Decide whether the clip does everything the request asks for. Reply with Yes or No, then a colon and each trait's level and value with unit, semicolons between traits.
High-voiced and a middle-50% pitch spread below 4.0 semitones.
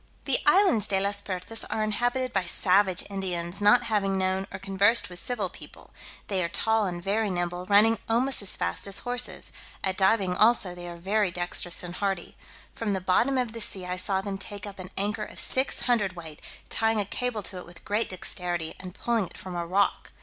Yes: high, 195 Hz; average, 3.3 semitones